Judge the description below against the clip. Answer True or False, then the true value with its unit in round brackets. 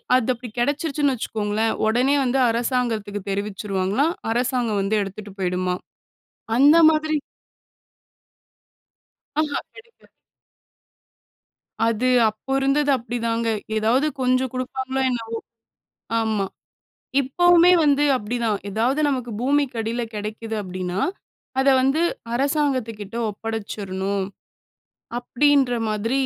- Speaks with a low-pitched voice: False (235 Hz)